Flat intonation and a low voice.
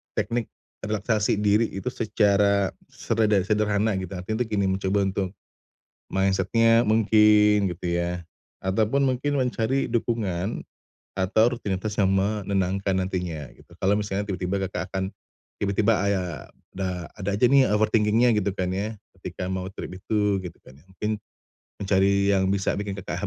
Yes: narrow, 2.3 semitones; low, 100 Hz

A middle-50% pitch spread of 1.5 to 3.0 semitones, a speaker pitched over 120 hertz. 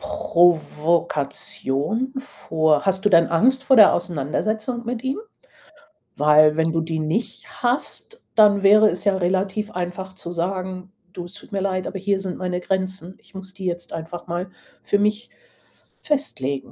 No: average, 3.7 semitones; medium, 185 Hz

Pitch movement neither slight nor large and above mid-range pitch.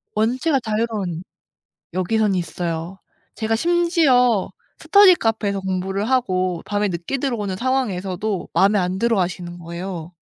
Yes: average, 4.6 semitones; high, 200 Hz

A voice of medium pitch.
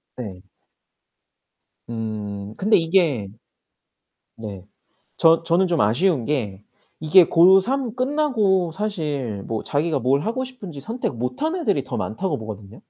Yes: medium, 160 Hz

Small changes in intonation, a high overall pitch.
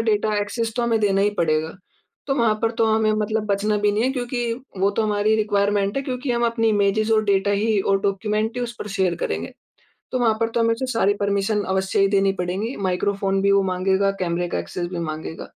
Yes: narrow, 2.3 semitones; high, 205 Hz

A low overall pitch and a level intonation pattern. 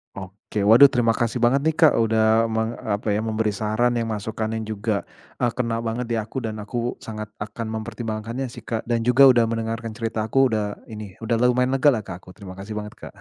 Yes: low, 115 Hz; narrow, 1.8 semitones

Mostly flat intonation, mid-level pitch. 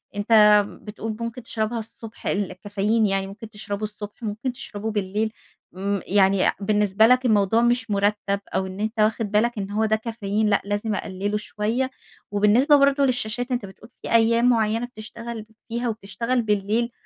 No: narrow, 2.2 semitones; high, 215 Hz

